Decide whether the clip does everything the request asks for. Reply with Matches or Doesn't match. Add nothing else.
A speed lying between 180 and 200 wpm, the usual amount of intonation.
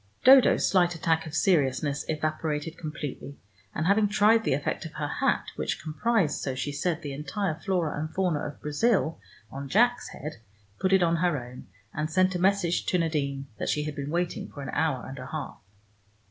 Matches